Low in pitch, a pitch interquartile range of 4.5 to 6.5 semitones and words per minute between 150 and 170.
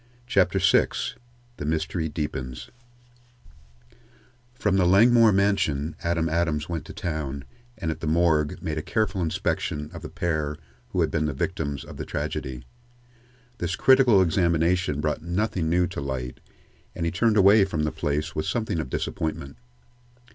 No: very low, 80 Hz; average, 3.8 semitones; average, 155 wpm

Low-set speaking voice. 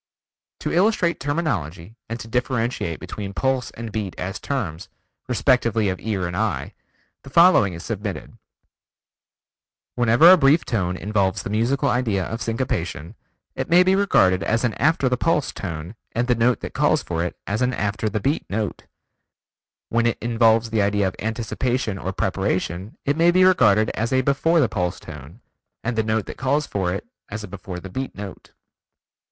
Yes: low, 110 Hz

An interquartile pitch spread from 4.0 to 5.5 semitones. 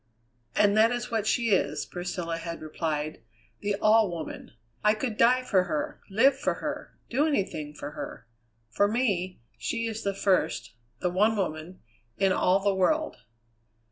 Yes: average, 4.7 semitones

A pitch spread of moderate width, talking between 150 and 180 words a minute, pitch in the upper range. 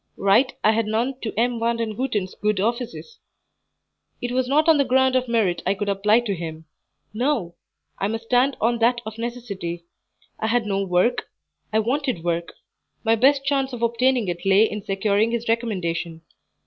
Yes: average, 3.8 semitones; average, 175 wpm; high, 225 Hz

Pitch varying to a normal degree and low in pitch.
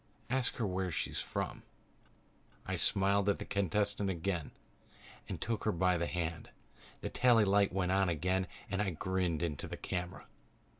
No: narrow, 2.3 semitones; very low, 95 Hz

